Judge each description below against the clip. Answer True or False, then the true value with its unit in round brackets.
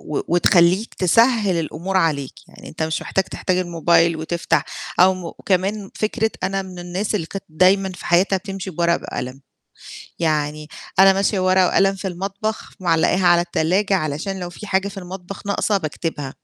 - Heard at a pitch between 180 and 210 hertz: True (185 Hz)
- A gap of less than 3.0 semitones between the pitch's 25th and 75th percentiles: True (2.6 semitones)